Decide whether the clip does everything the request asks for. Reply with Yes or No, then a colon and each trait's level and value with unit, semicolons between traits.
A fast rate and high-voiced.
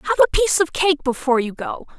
Yes: fast, 240 wpm; very high, 295 Hz